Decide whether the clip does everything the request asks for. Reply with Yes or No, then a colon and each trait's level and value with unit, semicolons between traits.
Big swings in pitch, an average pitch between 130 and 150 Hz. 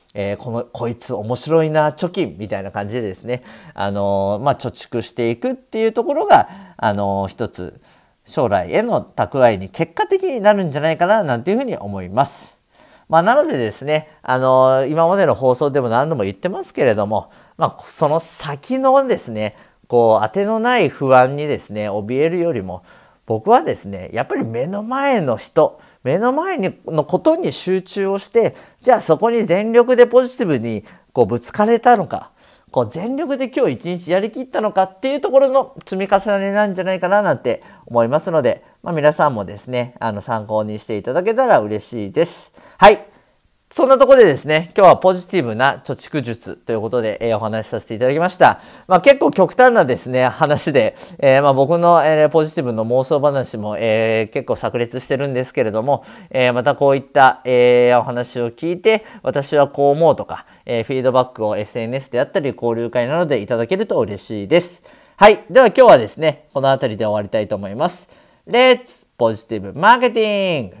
Yes: wide, 8.8 semitones; medium, 140 Hz